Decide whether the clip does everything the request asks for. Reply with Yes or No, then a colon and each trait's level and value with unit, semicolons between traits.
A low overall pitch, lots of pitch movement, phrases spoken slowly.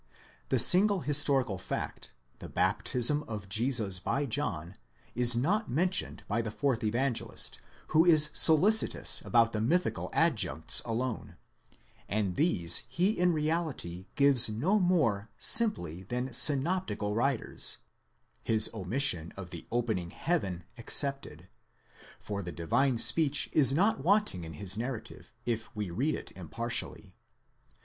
Yes: low, 125 Hz; wide, 6.7 semitones; slow, 130 wpm